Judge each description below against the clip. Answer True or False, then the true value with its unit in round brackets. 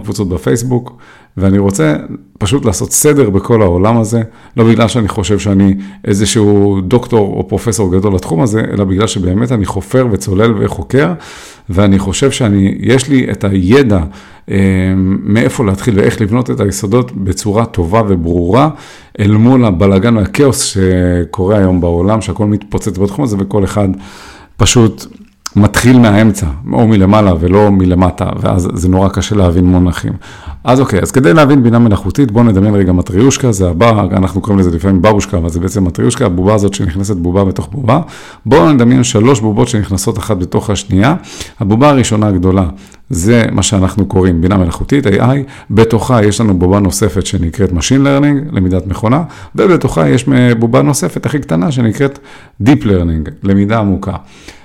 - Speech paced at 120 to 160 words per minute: True (145 wpm)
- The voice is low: True (105 Hz)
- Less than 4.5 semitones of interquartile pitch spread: True (3.8 semitones)